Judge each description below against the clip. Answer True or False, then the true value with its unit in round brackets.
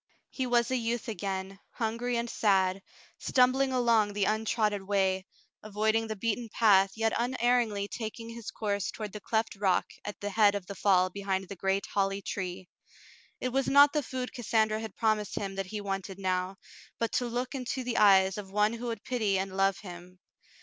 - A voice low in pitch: False (210 Hz)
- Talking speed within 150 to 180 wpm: False (190 wpm)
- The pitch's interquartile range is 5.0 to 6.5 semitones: False (3.2 semitones)